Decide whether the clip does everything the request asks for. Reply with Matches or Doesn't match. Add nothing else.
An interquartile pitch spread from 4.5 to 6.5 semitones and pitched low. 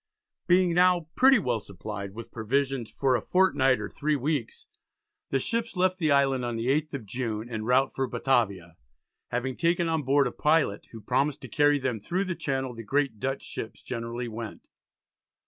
Matches